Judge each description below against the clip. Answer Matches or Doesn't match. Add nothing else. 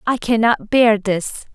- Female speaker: Matches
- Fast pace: Doesn't match